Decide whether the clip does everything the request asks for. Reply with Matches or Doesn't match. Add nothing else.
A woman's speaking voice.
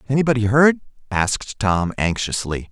Doesn't match